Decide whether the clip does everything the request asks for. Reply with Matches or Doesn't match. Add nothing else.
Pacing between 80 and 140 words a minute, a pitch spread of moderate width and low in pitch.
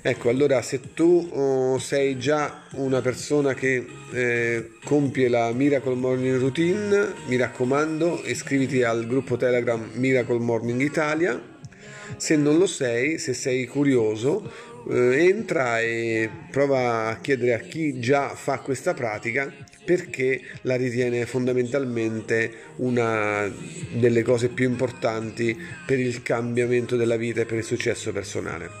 Matches